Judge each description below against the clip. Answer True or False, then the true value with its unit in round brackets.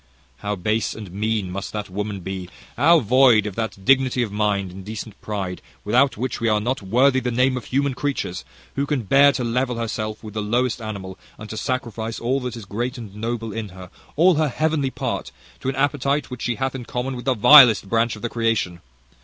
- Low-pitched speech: True (115 Hz)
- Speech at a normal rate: False (215 wpm)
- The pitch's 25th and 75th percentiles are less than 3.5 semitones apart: False (3.8 semitones)